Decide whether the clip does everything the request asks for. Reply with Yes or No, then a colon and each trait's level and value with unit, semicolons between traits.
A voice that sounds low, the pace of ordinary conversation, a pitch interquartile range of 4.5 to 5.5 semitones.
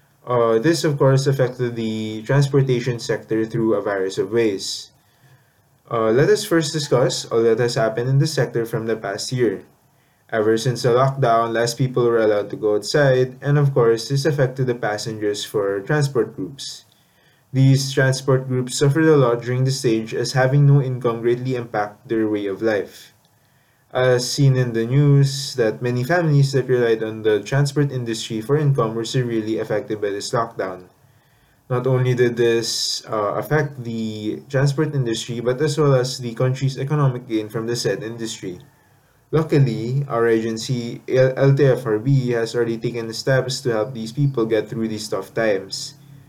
No: low, 125 Hz; average, 165 wpm; average, 3.3 semitones